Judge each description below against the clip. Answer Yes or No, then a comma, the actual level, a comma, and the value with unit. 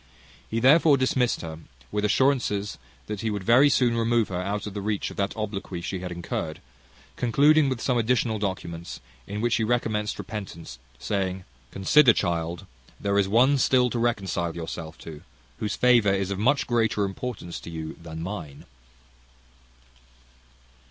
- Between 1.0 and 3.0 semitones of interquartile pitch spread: No, average, 4.5 semitones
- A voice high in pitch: No, low, 105 Hz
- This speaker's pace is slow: No, average, 160 wpm